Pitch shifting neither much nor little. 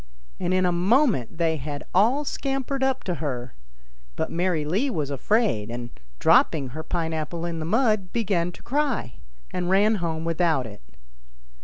No: wide, 5.8 semitones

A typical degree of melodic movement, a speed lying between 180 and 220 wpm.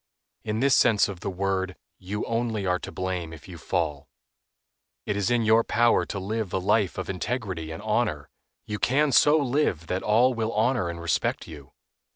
Yes: average, 4.3 semitones; average, 190 wpm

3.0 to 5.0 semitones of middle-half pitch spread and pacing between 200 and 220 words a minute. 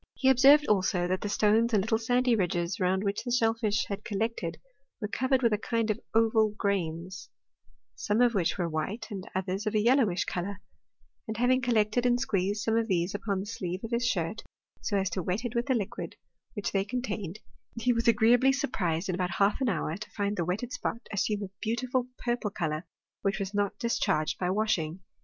Yes: average, 3.7 semitones; fast, 205 wpm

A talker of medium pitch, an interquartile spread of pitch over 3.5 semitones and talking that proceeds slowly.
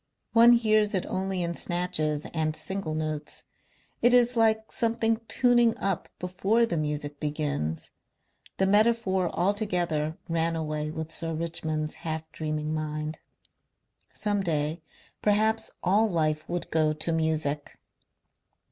Yes: medium, 170 Hz; average, 5.2 semitones; slow, 125 wpm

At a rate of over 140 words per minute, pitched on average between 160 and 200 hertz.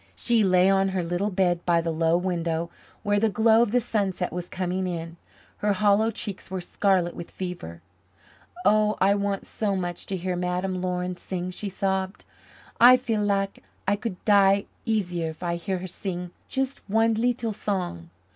Yes: average, 175 wpm; high, 190 Hz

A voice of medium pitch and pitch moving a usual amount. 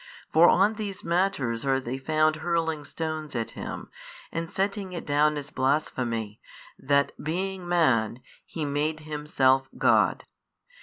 Yes: medium, 155 Hz; average, 4.1 semitones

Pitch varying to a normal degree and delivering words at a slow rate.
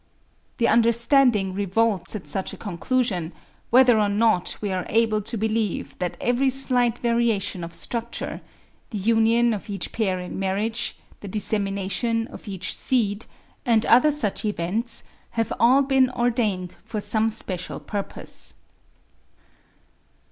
Yes: average, 3.1 semitones; slow, 125 wpm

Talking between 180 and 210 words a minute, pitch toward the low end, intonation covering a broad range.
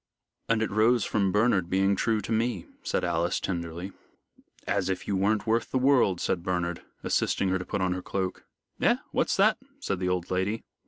No: average, 195 wpm; very low, 95 Hz; average, 3.2 semitones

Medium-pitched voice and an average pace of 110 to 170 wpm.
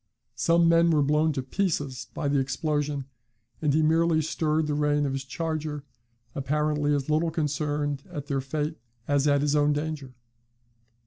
Yes: medium, 150 Hz; average, 165 wpm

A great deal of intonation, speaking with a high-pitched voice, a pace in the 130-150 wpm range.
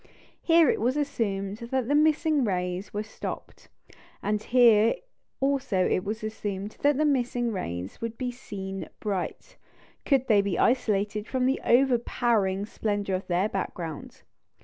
No: average, 4.6 semitones; high, 220 Hz; average, 145 wpm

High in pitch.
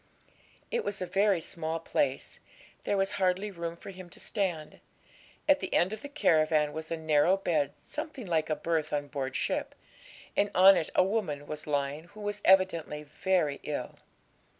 No: medium, 170 Hz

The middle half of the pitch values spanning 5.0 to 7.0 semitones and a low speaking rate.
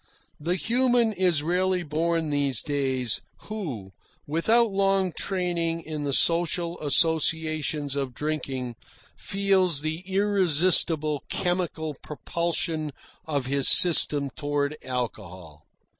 No: average, 4.0 semitones; slow, 100 wpm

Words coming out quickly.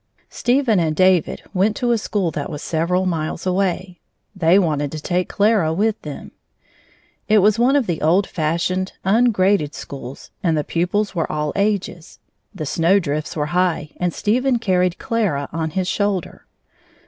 No: average, 160 wpm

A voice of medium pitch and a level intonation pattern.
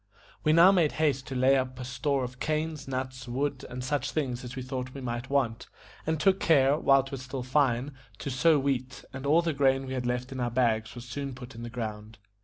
No: low, 130 Hz; narrow, 2.3 semitones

